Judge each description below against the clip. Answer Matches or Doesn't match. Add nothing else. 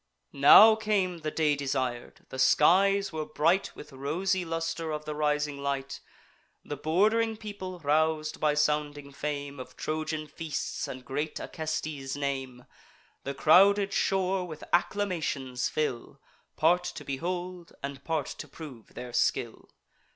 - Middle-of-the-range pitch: Matches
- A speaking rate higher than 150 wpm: Doesn't match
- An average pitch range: Matches